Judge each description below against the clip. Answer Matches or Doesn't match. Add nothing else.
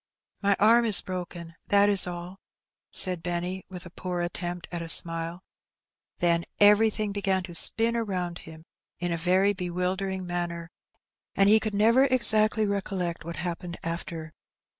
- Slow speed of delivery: Doesn't match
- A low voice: Doesn't match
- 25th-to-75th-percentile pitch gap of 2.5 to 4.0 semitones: Matches